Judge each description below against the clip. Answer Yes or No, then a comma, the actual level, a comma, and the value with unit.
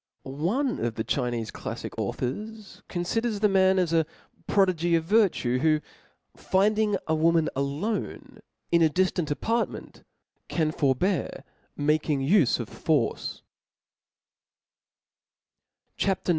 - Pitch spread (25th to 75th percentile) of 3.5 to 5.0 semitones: No, wide, 5.4 semitones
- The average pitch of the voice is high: No, medium, 170 Hz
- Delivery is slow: Yes, slow, 115 wpm